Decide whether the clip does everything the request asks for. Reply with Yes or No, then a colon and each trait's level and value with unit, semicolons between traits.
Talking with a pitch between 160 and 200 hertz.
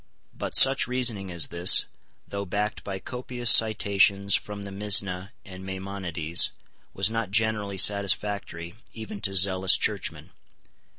No: low, 100 Hz